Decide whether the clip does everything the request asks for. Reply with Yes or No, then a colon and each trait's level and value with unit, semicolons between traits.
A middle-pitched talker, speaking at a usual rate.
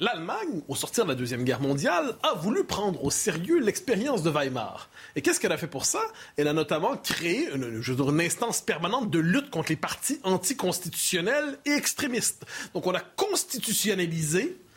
Yes: medium, 180 Hz; average, 175 wpm